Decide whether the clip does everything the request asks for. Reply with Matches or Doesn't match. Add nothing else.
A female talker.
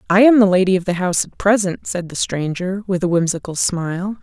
Matches